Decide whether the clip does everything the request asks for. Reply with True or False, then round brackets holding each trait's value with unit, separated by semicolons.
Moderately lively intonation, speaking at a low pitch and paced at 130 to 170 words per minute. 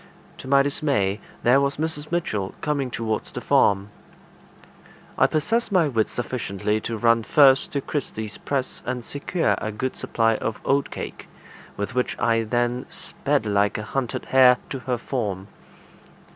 True (4.3 semitones; 125 Hz; 150 wpm)